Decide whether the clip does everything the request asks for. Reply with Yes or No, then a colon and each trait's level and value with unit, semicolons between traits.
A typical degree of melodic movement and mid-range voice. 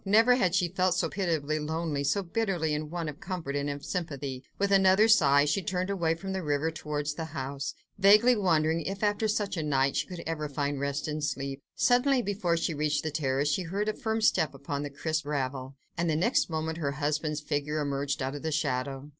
Yes: average, 4.6 semitones; medium, 155 Hz